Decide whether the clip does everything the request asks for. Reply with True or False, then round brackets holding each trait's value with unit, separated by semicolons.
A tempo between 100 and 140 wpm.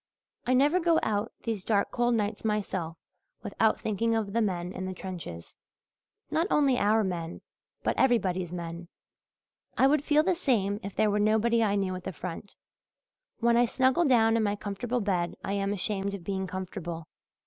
False (180 wpm)